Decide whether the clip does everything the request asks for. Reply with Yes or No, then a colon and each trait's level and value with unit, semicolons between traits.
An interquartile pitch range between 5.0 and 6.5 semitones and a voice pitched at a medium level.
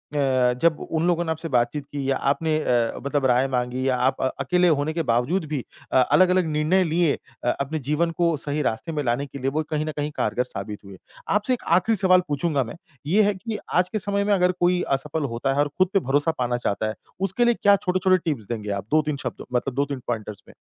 Yes: wide, 5.4 semitones; medium, 150 Hz